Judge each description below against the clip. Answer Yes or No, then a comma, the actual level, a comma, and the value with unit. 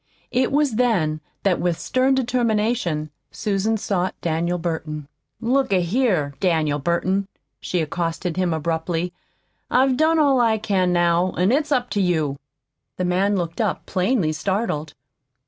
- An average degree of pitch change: No, wide, 5.8 semitones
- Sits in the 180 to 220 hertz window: Yes, medium, 185 Hz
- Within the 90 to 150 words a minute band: Yes, average, 145 wpm